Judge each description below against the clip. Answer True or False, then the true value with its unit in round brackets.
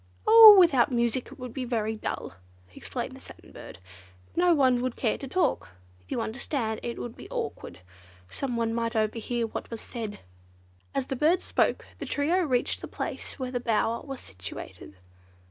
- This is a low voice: False (245 Hz)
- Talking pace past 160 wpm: True (170 wpm)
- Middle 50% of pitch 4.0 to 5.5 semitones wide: False (3.3 semitones)